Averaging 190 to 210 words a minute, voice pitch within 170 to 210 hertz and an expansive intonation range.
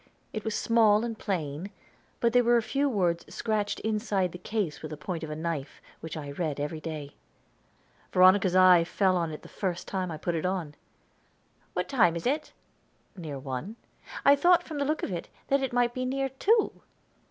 Yes: average, 200 wpm; medium, 185 Hz; wide, 6.4 semitones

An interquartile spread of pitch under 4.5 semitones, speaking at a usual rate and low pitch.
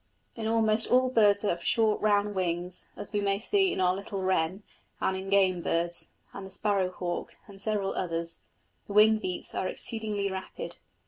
No: narrow, 2.6 semitones; average, 185 wpm; high, 200 Hz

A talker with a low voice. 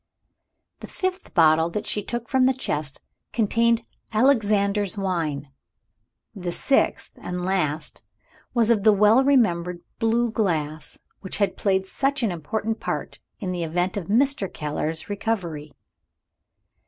No: high, 200 Hz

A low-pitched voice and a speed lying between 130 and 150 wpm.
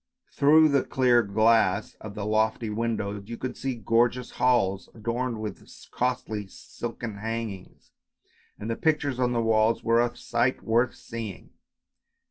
Yes: low, 115 Hz; average, 140 wpm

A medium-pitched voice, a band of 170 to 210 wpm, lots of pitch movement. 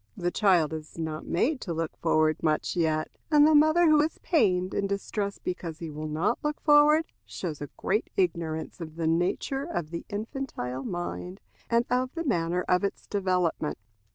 Yes: medium, 180 Hz; average, 180 wpm; wide, 7.8 semitones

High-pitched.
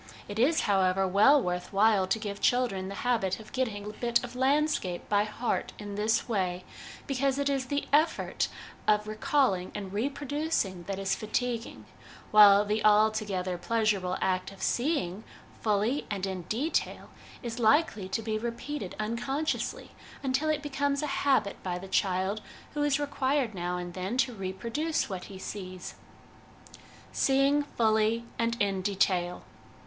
Yes: high, 215 Hz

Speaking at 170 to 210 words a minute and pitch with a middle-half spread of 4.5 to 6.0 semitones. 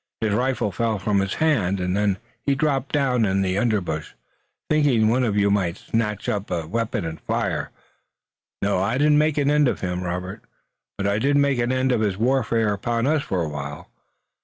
Yes: average, 200 wpm; average, 5.2 semitones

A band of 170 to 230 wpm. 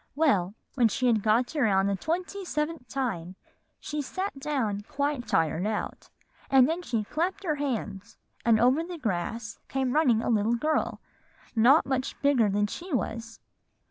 No: average, 160 wpm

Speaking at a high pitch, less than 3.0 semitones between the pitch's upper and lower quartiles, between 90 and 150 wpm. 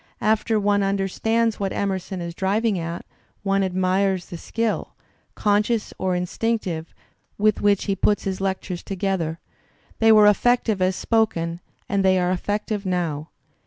Yes: high, 195 Hz; narrow, 2.4 semitones; average, 140 wpm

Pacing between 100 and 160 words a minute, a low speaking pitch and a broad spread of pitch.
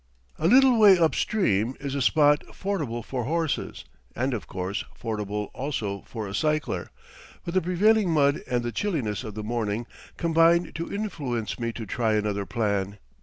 No: average, 170 wpm; low, 130 Hz; wide, 7.5 semitones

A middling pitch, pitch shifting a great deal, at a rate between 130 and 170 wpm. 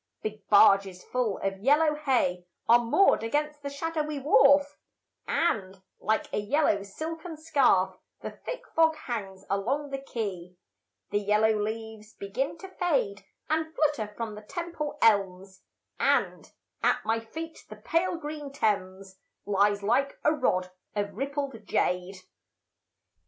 No: high, 230 Hz; wide, 6.9 semitones; slow, 135 wpm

